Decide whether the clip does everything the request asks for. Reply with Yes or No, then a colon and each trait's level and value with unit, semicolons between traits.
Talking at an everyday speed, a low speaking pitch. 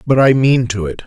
No: fast, 280 wpm; low, 120 Hz